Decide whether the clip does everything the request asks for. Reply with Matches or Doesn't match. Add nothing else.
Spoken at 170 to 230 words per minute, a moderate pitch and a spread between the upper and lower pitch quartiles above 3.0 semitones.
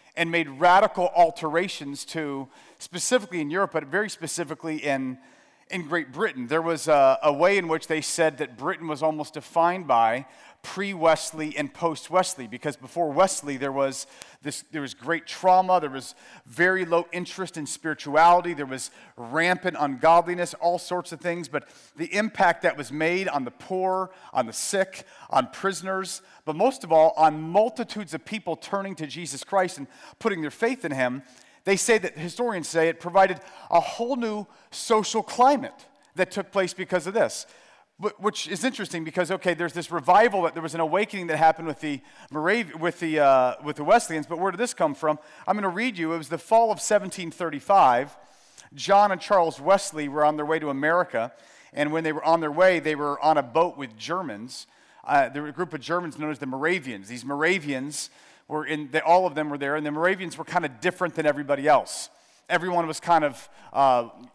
Matches